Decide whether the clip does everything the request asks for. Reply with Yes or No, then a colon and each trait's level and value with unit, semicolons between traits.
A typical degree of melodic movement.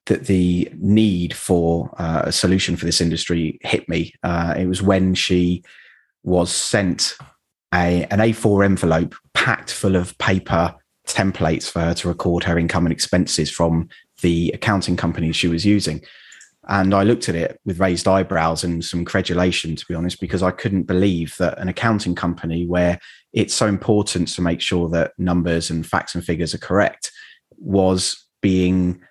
No: narrow, 2.1 semitones